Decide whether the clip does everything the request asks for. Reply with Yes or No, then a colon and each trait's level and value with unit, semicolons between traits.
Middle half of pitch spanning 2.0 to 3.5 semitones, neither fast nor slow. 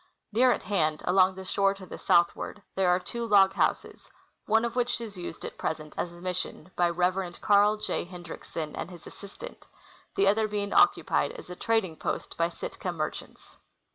Yes: average, 3.1 semitones; average, 185 wpm